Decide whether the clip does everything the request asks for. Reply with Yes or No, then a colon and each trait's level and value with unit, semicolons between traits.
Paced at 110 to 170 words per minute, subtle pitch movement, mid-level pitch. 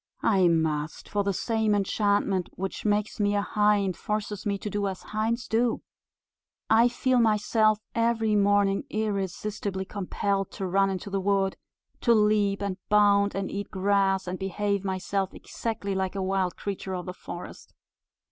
No: average, 155 wpm; narrow, 1.6 semitones; high, 200 Hz